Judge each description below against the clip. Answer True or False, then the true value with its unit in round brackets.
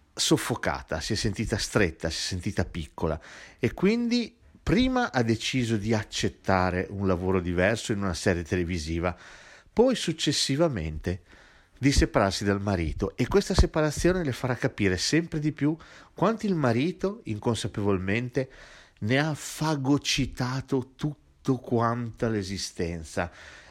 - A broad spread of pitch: True (7.6 semitones)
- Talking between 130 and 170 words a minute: False (120 wpm)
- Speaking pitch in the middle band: False (115 Hz)